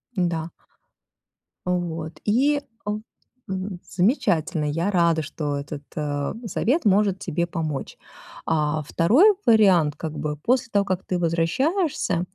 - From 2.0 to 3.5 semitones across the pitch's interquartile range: No, average, 4.8 semitones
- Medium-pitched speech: Yes, medium, 175 Hz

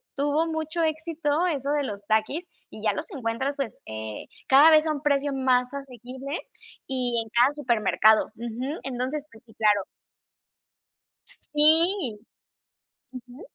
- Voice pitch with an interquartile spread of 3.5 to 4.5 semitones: Yes, average, 4.2 semitones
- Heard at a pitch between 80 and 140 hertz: No, very high, 270 Hz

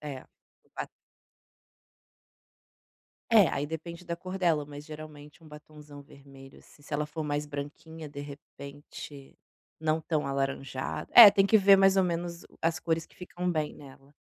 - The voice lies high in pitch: No, medium, 150 Hz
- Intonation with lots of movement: No, average, 2.9 semitones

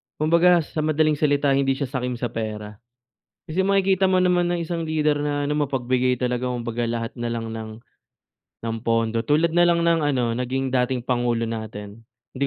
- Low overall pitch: Yes, low, 130 Hz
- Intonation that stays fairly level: No, average, 5.0 semitones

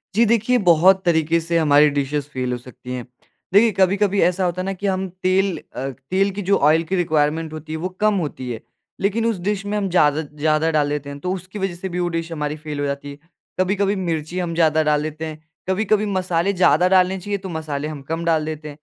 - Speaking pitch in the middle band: Yes, medium, 170 Hz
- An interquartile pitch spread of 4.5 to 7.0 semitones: No, average, 4.1 semitones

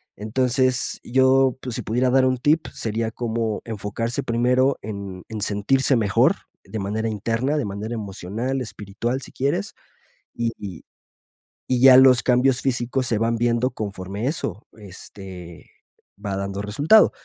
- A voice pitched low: Yes, low, 115 Hz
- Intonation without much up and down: No, average, 3.8 semitones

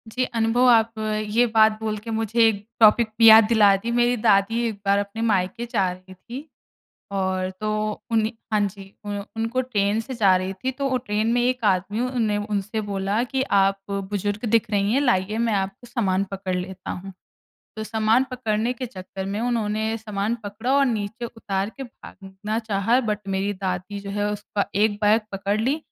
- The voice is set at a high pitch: Yes, high, 215 Hz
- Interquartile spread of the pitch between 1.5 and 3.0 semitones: Yes, narrow, 2.6 semitones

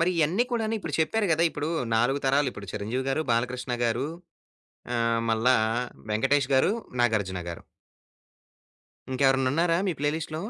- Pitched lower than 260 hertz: Yes, low, 135 Hz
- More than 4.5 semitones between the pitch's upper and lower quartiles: Yes, average, 5.2 semitones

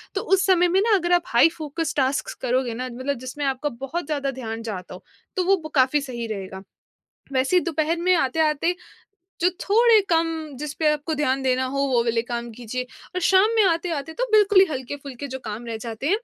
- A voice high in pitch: Yes, very high, 285 Hz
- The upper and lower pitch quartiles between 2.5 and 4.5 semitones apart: No, wide, 5.5 semitones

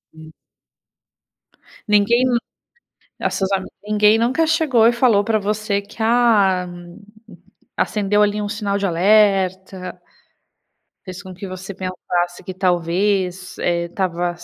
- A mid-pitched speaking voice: No, high, 200 Hz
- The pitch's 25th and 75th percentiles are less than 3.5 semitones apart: Yes, narrow, 2.6 semitones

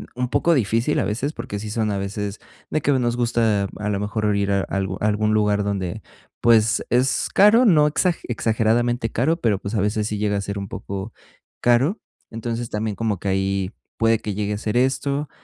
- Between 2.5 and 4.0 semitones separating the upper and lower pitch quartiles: Yes, average, 2.9 semitones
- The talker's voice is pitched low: Yes, low, 110 Hz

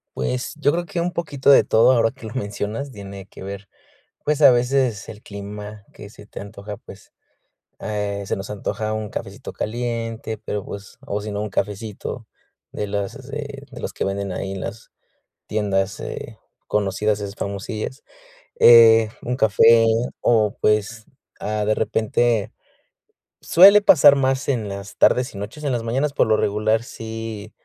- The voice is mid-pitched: No, low, 110 Hz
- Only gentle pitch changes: No, average, 3.1 semitones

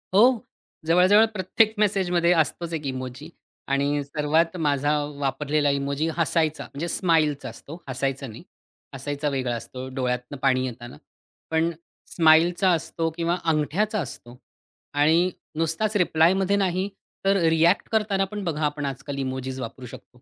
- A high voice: No, medium, 155 Hz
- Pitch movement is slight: No, average, 4.2 semitones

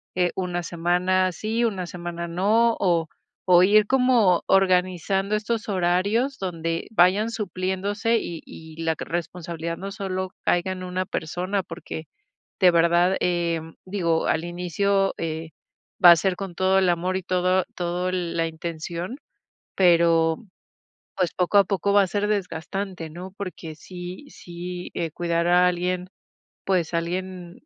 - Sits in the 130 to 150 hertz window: No, medium, 180 Hz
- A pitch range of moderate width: No, narrow, 2.1 semitones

